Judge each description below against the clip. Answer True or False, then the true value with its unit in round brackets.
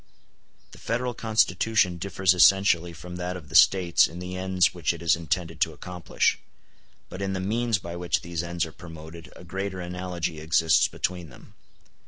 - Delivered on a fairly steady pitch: True (2.0 semitones)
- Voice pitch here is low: True (90 Hz)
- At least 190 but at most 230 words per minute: False (175 wpm)